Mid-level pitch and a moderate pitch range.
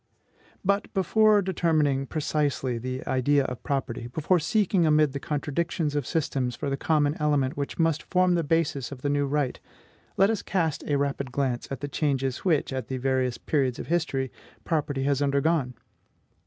Yes: medium, 145 Hz; average, 3.4 semitones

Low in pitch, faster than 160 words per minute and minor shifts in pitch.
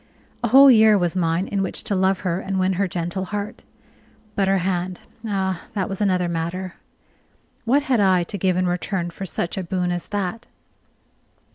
No: high, 190 Hz; average, 185 wpm; narrow, 2.1 semitones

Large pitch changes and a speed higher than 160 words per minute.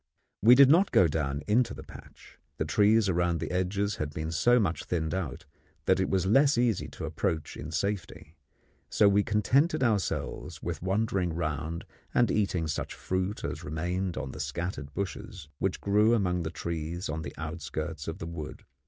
No: average, 4.7 semitones; average, 180 wpm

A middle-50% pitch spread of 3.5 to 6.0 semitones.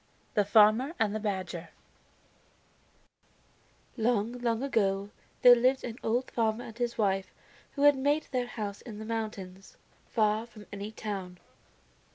No: average, 3.0 semitones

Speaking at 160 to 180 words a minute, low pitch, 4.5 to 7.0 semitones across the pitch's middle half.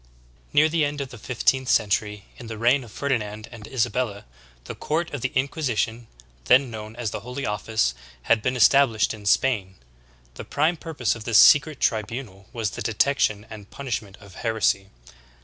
No: average, 175 wpm; low, 115 Hz; average, 4.1 semitones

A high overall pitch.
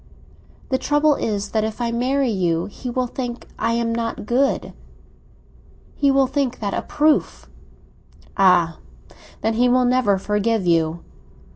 Yes: high, 235 Hz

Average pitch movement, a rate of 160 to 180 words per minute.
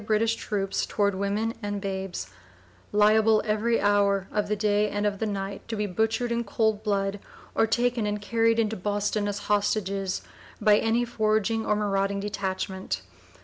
No: narrow, 1.7 semitones; average, 165 wpm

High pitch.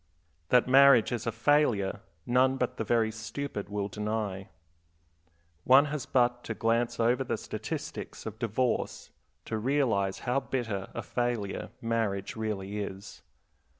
No: low, 115 Hz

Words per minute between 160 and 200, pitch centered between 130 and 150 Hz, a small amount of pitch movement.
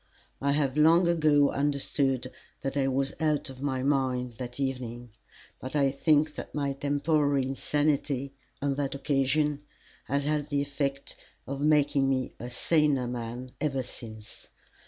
No: average, 140 wpm; medium, 140 Hz; narrow, 1.9 semitones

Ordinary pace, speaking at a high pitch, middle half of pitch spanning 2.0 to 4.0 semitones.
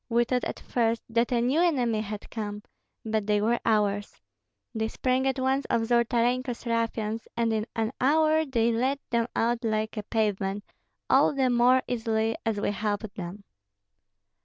Yes: average, 165 wpm; high, 230 Hz; narrow, 2.5 semitones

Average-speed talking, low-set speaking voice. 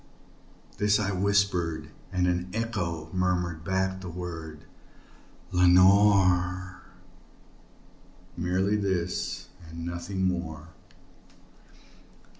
No: slow, 75 wpm; very low, 90 Hz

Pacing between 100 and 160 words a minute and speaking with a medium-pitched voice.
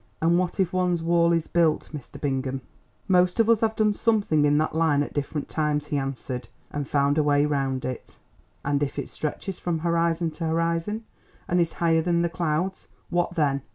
No: average, 195 wpm; medium, 165 Hz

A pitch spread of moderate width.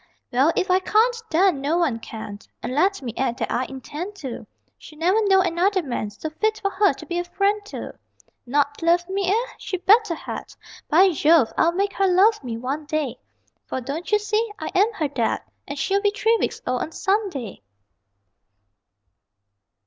No: wide, 6.1 semitones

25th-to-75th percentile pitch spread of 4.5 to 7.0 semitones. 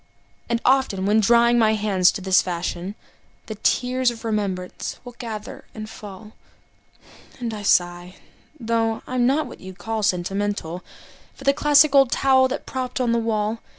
No: average, 3.9 semitones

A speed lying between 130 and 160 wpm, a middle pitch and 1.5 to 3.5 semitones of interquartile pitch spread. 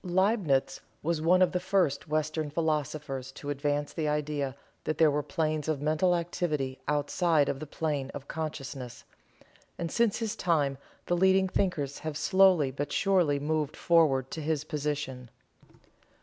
Yes: average, 150 wpm; medium, 155 Hz; average, 3.2 semitones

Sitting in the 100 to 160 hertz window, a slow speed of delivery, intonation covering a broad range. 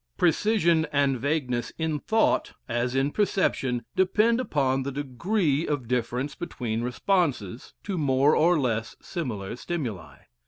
Yes: medium, 140 Hz; slow, 125 wpm; wide, 5.7 semitones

